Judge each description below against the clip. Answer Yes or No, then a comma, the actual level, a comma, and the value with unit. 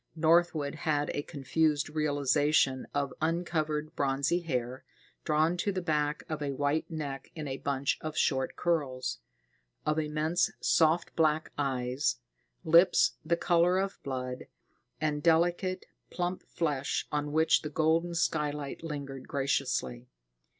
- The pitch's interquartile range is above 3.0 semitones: No, average, 2.7 semitones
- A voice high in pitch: No, medium, 150 Hz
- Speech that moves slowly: Yes, slow, 130 wpm